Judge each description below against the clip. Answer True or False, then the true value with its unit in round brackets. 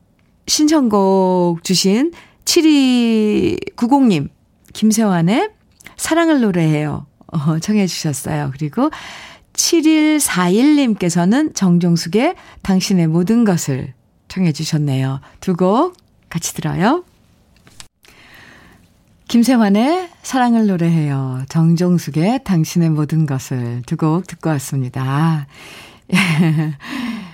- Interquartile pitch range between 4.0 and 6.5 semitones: False (7.2 semitones)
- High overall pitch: False (180 Hz)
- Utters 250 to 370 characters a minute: False (190 characters per minute)